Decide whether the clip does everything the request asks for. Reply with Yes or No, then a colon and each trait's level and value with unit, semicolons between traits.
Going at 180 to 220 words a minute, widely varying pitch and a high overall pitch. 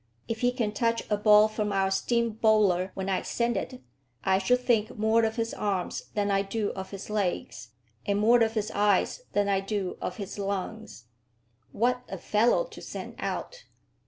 No: average, 190 wpm; average, 2.7 semitones; high, 210 Hz